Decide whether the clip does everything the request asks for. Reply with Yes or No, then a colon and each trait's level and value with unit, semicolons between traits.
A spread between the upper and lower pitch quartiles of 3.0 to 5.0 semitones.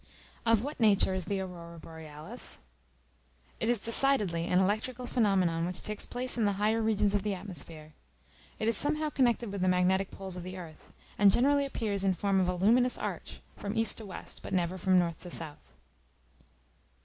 Yes: average, 3.9 semitones